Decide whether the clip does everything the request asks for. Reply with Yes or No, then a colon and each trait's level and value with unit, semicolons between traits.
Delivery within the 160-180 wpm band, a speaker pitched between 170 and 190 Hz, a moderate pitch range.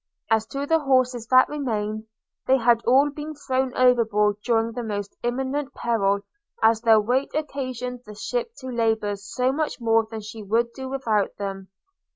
No: average, 170 wpm; high, 235 Hz; average, 3.3 semitones